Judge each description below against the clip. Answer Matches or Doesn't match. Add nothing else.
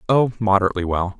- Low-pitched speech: Matches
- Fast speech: Doesn't match